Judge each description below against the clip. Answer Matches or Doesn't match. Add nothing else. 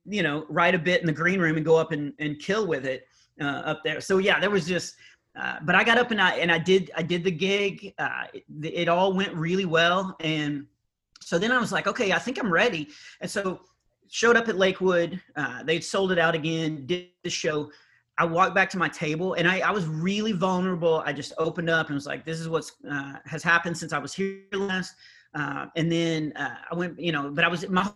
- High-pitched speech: Doesn't match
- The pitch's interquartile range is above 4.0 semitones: Doesn't match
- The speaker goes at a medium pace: Doesn't match